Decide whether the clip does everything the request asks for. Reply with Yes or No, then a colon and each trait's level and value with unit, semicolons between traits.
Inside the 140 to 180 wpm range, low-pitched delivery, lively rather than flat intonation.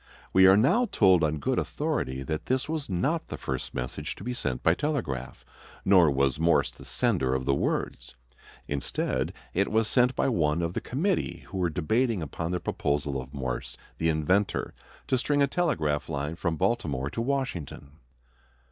Yes: average, 175 wpm; very low, 85 Hz; wide, 9.0 semitones